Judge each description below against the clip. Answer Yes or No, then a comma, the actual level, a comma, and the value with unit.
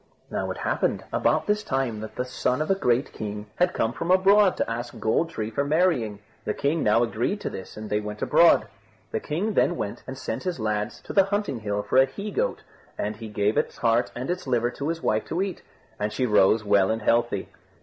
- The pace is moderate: No, fast, 230 wpm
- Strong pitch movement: Yes, wide, 7.8 semitones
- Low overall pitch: Yes, low, 120 Hz